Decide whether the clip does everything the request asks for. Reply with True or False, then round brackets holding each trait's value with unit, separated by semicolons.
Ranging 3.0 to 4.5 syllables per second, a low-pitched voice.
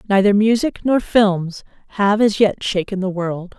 False (4.2 syllables/s; 200 Hz)